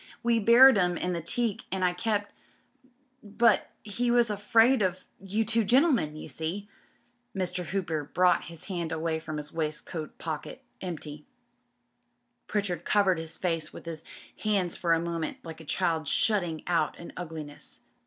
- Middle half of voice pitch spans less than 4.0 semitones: No, average, 4.4 semitones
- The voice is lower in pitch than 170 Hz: No, medium, 180 Hz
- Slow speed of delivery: No, average, 165 wpm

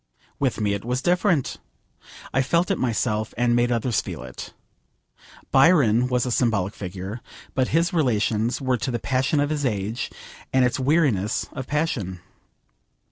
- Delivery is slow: No, average, 155 wpm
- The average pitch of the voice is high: No, low, 125 Hz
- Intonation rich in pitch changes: No, average, 4.5 semitones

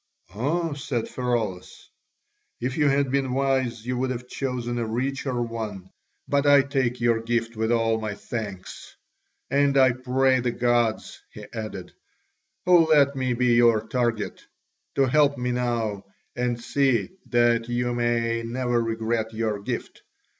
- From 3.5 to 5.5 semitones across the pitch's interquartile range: No, narrow, 2.4 semitones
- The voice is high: No, low, 120 Hz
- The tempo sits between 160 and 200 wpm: No, average, 145 wpm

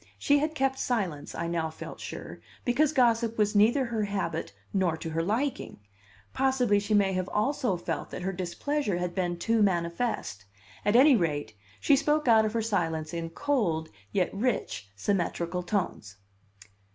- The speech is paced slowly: No, average, 165 wpm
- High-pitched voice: Yes, high, 205 Hz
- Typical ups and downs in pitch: No, wide, 6.1 semitones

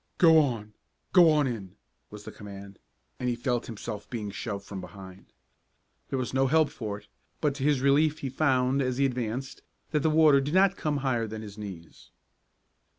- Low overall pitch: Yes, low, 125 Hz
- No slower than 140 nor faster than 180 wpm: No, average, 190 wpm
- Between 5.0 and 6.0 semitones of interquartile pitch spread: Yes, wide, 5.6 semitones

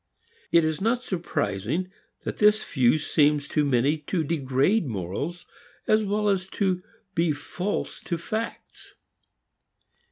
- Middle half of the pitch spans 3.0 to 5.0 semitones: No, wide, 5.4 semitones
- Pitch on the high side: No, medium, 165 Hz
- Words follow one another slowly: Yes, slow, 125 wpm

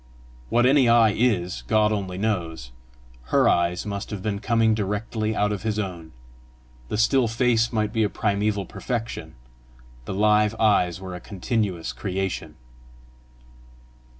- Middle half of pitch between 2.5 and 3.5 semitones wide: Yes, average, 2.9 semitones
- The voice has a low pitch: Yes, low, 105 Hz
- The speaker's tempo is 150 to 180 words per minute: No, average, 140 wpm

